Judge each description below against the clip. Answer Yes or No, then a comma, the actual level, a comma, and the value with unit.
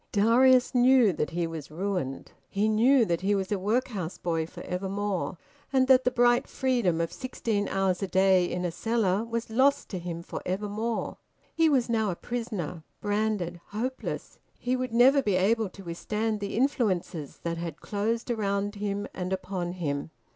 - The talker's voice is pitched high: Yes, high, 205 Hz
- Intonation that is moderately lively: Yes, average, 4.5 semitones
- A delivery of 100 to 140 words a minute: No, average, 175 wpm